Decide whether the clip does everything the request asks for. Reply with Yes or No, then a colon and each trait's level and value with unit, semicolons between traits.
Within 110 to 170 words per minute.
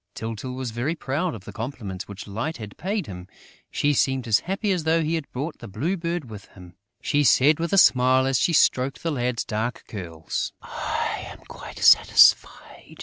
No: average, 195 wpm